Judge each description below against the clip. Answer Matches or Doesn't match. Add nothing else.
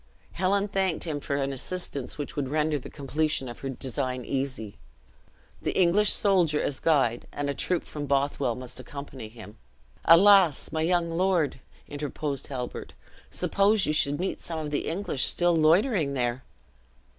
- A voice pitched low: Doesn't match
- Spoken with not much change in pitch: Doesn't match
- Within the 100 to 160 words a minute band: Matches